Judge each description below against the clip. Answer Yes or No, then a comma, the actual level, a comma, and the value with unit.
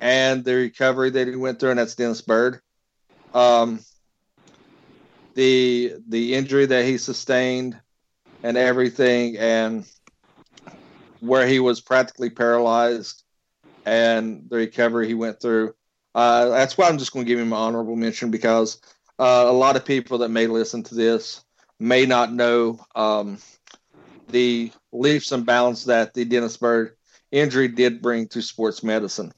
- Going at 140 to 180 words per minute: Yes, average, 150 wpm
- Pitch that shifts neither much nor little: No, narrow, 1.9 semitones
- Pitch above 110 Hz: Yes, low, 120 Hz